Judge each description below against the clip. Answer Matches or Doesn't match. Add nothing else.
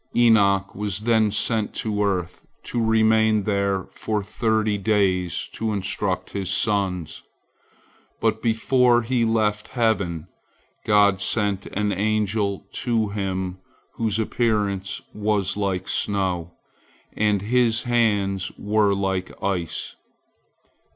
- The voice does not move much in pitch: Matches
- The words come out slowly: Matches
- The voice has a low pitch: Matches